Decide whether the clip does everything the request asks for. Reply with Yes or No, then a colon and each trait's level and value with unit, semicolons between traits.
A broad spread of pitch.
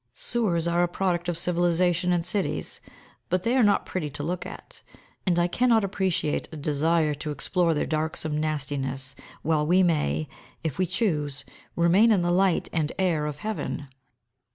No: average, 3.5 semitones